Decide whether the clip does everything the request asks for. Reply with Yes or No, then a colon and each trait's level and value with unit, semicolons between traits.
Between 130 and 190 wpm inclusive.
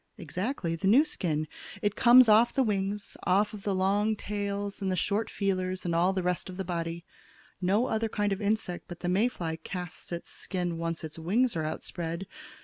No: fast, 205 wpm